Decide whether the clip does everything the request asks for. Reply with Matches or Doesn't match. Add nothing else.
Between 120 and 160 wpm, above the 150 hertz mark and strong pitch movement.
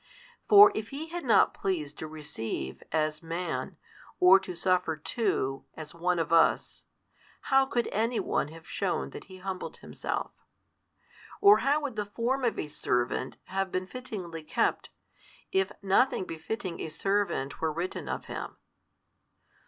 Matches